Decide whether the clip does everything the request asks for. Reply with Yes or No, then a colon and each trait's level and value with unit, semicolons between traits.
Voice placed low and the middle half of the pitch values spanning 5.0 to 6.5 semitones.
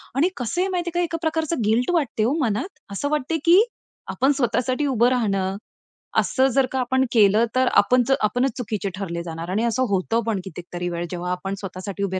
No: high, 230 Hz; wide, 5.6 semitones